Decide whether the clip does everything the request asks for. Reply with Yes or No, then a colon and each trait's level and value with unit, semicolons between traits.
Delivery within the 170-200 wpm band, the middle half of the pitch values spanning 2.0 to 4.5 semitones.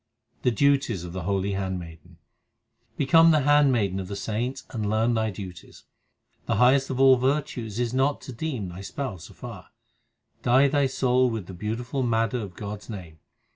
No: average, 175 wpm; average, 5.2 semitones